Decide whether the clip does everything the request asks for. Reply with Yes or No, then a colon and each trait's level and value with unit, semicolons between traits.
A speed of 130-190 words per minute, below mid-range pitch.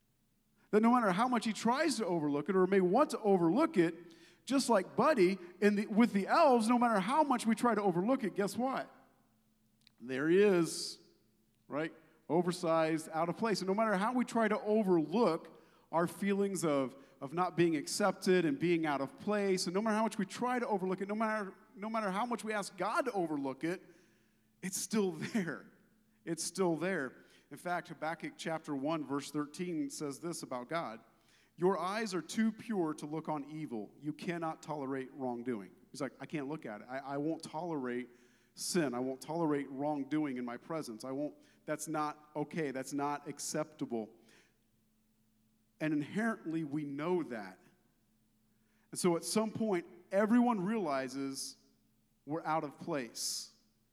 No: average, 175 wpm; medium, 165 Hz